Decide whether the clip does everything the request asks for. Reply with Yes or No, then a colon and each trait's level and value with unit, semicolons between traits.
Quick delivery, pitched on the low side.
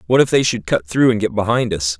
Yes: fast, 300 wpm; low, 110 Hz